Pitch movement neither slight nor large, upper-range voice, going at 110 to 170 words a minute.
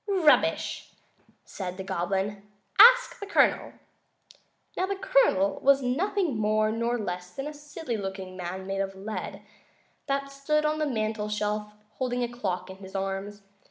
No: wide, 6.7 semitones; high, 215 Hz; average, 160 wpm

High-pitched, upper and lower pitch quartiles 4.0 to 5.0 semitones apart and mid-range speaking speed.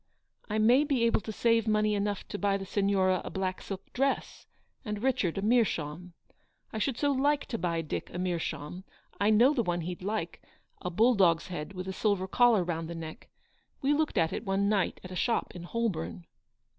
No: high, 200 Hz; average, 4.5 semitones; fast, 215 wpm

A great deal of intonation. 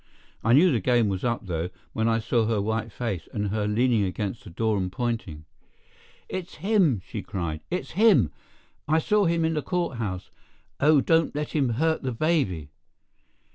Yes: wide, 7.5 semitones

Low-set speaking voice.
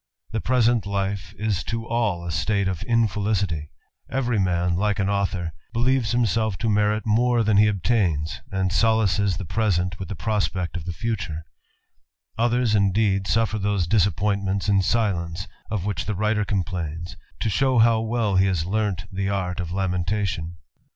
Yes: low, 100 Hz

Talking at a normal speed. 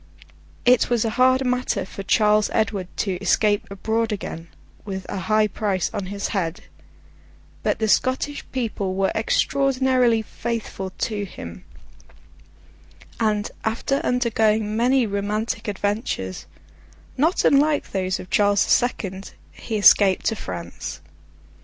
No: slow, 125 wpm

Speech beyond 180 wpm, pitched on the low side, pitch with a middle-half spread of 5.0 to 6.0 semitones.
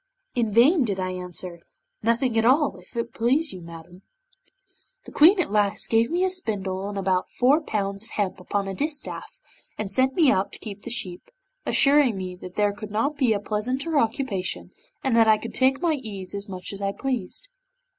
No: average, 200 wpm; high, 220 Hz; average, 5.3 semitones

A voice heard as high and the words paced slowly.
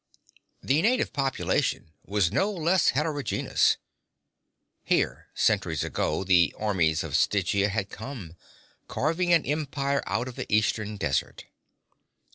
No: low, 115 Hz; slow, 115 wpm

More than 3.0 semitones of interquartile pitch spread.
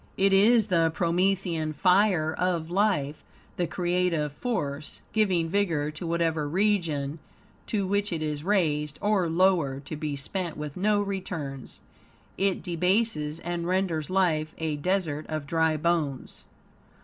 Yes: average, 3.9 semitones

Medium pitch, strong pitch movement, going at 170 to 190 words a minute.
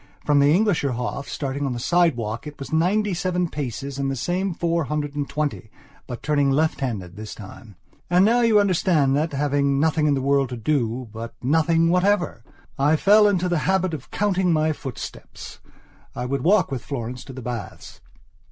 No: medium, 145 Hz; average, 4.8 semitones; average, 180 wpm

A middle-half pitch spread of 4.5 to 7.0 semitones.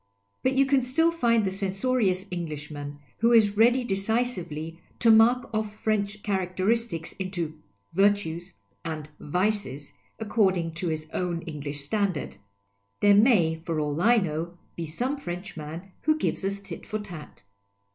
Yes: average, 5.3 semitones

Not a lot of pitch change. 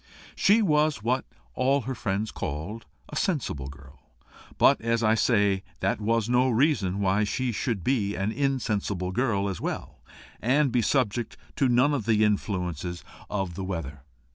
No: average, 4.9 semitones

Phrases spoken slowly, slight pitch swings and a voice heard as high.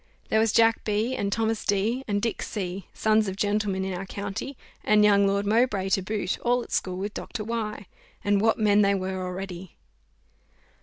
No: average, 190 wpm; narrow, 2.2 semitones; high, 205 Hz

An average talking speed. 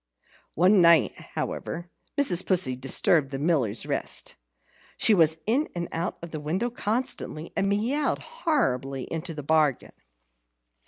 No: slow, 130 wpm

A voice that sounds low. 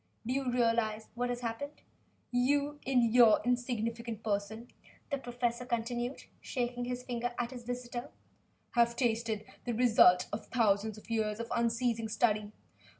No: high, 235 Hz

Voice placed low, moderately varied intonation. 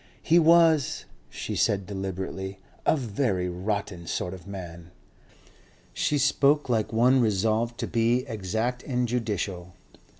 Yes: low, 110 Hz; average, 4.7 semitones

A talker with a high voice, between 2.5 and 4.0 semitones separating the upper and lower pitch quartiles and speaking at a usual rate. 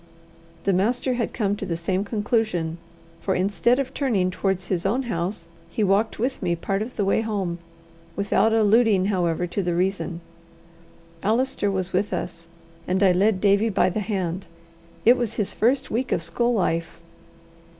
Yes: high, 200 Hz; average, 3.6 semitones; average, 170 wpm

